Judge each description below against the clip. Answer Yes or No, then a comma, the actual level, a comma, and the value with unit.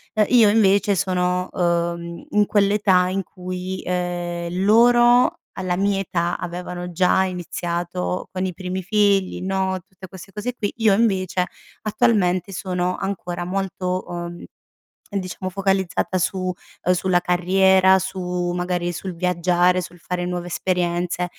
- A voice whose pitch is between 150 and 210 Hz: Yes, medium, 185 Hz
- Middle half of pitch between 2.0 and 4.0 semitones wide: No, narrow, 1.6 semitones